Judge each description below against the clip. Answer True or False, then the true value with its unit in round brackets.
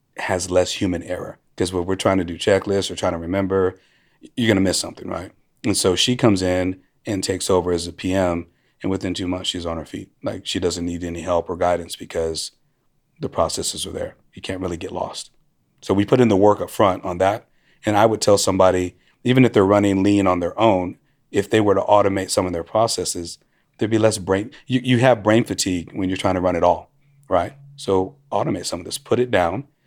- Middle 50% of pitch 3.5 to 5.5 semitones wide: False (2.7 semitones)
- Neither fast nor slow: False (230 wpm)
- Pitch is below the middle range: True (95 Hz)